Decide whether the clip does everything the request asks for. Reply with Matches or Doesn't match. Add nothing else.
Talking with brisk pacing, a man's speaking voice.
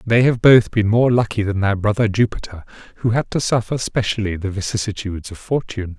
Doesn't match